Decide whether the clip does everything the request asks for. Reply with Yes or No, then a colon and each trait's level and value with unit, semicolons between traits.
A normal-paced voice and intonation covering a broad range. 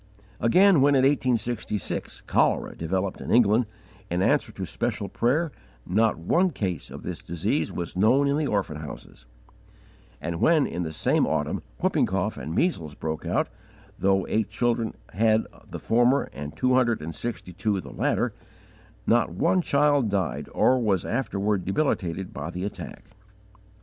Yes: average, 155 wpm; wide, 6.1 semitones